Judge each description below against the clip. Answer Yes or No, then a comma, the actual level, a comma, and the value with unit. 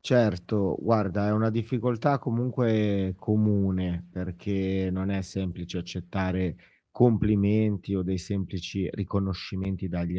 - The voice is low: Yes, very low, 95 Hz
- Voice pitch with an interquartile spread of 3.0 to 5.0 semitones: No, narrow, 2.6 semitones